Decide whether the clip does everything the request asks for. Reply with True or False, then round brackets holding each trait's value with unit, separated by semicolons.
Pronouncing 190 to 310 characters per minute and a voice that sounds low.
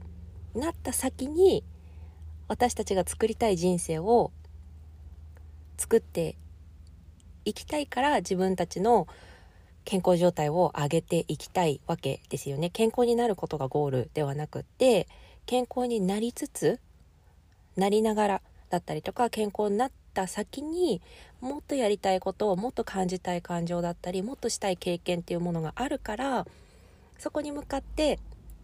False (290 characters per minute; 185 Hz)